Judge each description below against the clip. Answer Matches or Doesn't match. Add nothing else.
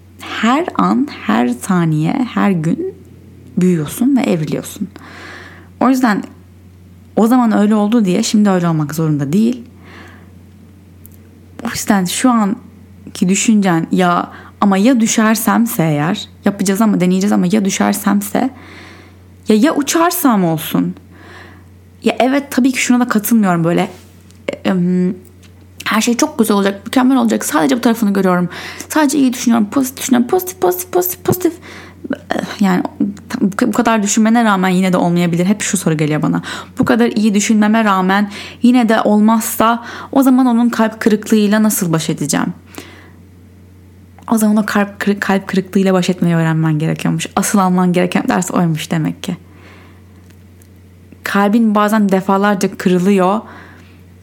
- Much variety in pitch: Matches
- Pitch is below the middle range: Doesn't match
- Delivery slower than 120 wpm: Doesn't match